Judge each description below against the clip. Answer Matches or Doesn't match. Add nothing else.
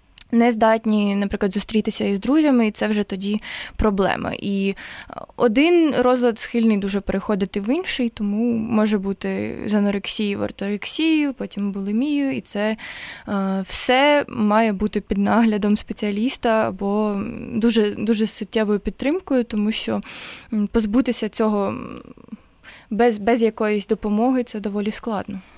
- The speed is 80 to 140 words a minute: Matches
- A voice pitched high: Matches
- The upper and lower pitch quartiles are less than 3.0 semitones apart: Matches